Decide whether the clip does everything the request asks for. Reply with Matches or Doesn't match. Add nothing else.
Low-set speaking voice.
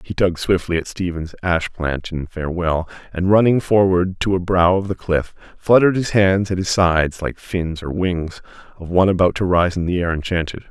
Matches